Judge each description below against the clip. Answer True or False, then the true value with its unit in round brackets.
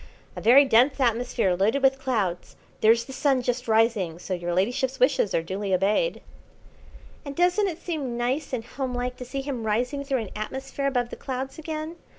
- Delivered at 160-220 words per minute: True (180 wpm)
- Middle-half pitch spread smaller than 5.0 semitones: True (3.8 semitones)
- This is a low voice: False (250 Hz)